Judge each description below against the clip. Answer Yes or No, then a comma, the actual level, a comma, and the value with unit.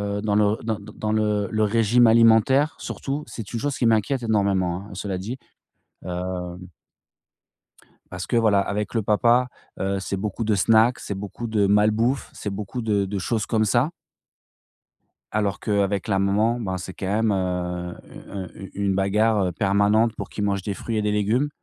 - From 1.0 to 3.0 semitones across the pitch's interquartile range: Yes, narrow, 2.4 semitones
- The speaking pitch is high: No, low, 105 Hz